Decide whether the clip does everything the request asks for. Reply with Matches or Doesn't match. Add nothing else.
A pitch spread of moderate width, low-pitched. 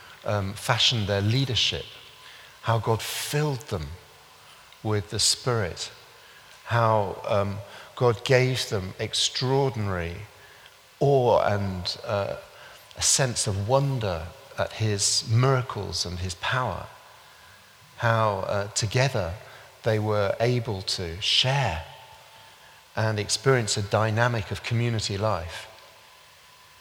Matches